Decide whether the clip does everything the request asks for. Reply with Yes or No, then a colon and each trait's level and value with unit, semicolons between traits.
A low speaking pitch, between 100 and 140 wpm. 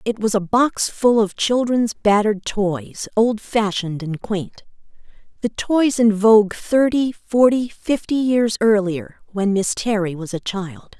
No: high, 210 Hz; slow, 135 wpm